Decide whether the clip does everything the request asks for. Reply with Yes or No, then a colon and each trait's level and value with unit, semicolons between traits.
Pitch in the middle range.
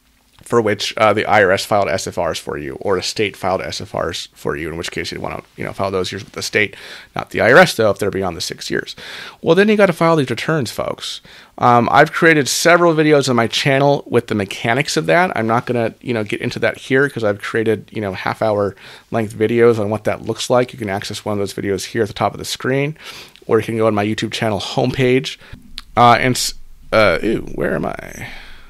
No: low, 115 Hz